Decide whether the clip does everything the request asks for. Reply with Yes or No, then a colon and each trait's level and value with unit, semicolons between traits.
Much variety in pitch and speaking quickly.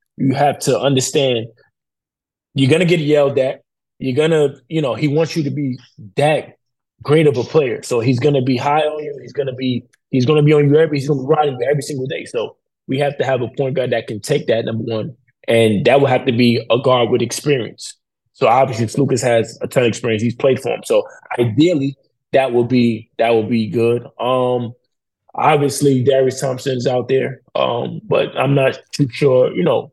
No: average, 3.3 semitones; fast, 215 wpm